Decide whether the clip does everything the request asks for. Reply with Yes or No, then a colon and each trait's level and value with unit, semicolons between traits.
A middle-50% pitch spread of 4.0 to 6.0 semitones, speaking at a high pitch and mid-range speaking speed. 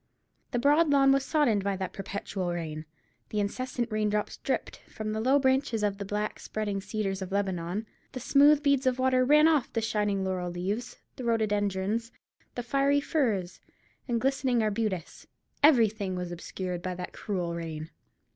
Yes: average, 5.2 semitones; high, 215 Hz; average, 165 wpm